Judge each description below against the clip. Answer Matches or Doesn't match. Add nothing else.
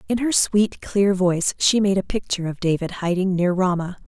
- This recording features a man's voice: Doesn't match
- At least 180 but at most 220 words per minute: Matches